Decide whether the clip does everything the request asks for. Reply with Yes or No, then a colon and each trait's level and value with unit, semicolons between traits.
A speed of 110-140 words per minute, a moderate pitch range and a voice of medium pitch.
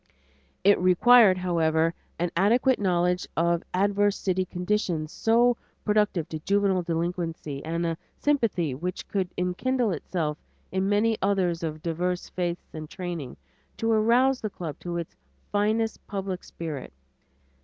Yes: slow, 135 wpm; average, 3.6 semitones; medium, 180 Hz